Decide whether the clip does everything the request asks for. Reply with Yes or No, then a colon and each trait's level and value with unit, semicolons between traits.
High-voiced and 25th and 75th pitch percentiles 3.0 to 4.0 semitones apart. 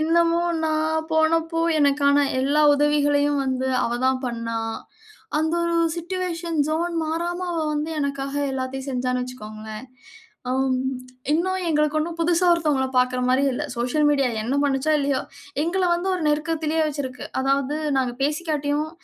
Yes: very high, 295 Hz; average, 3.6 semitones